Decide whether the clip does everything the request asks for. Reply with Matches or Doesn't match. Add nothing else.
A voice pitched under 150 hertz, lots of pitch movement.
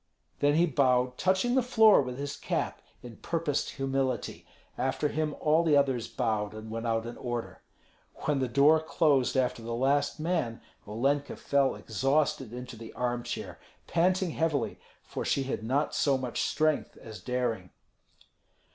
Doesn't match